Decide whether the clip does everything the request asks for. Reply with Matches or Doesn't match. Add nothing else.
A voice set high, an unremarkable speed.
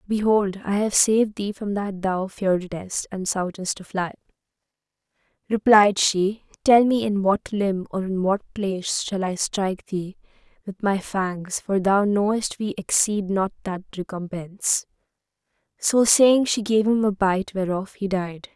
Matches